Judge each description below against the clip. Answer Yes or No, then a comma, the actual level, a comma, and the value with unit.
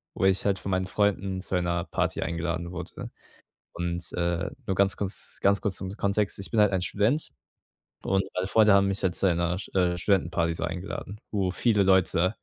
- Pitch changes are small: Yes, narrow, 2.2 semitones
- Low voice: Yes, very low, 95 Hz